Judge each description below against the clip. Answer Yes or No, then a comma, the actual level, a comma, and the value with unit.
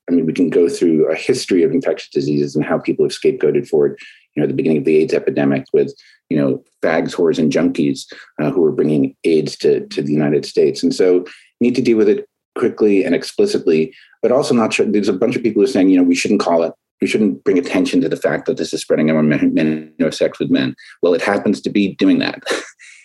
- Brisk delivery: Yes, fast, 255 wpm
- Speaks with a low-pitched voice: No, very high, 380 Hz